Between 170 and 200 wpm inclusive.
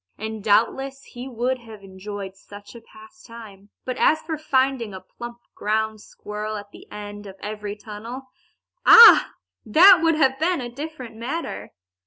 No: average, 155 wpm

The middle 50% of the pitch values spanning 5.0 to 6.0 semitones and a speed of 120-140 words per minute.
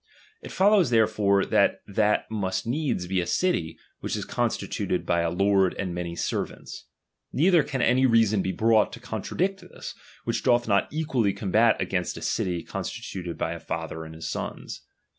No: wide, 5.5 semitones; average, 170 wpm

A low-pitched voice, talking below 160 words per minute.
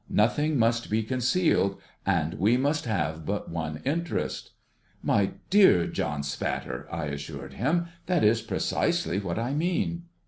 Yes: low, 110 Hz; average, 150 wpm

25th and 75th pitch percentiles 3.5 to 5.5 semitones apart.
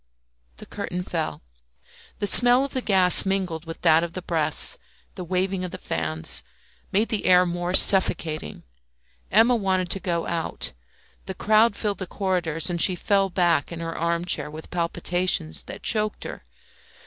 No: average, 2.7 semitones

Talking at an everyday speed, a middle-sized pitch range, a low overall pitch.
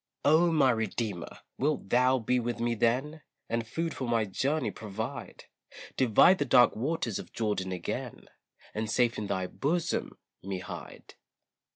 Yes: average, 150 wpm; average, 4.6 semitones; low, 120 Hz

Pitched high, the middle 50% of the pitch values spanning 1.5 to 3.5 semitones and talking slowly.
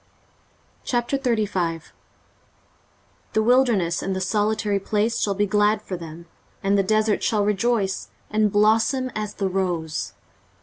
Yes: high, 210 Hz; narrow, 2.4 semitones; slow, 125 wpm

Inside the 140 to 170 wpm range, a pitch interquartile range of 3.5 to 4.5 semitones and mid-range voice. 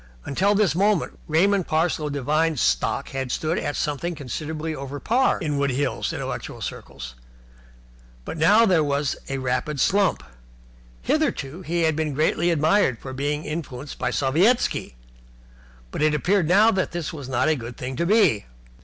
Yes: average, 160 wpm; average, 4.0 semitones; medium, 155 Hz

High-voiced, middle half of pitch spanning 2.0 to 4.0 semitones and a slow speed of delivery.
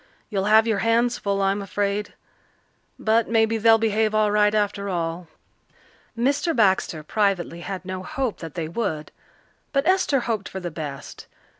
No: high, 205 Hz; average, 3.2 semitones; average, 155 wpm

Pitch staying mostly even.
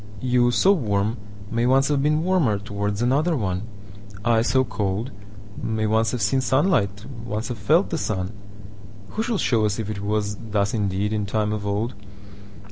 No: average, 3.6 semitones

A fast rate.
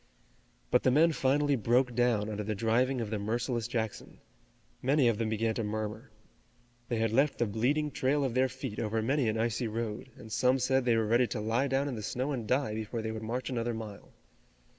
Yes: fast, 215 wpm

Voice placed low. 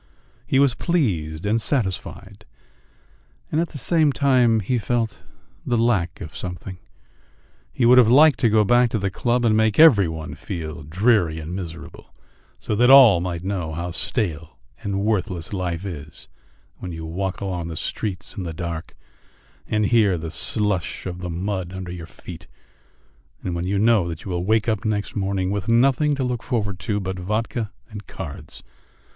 Yes: low, 100 Hz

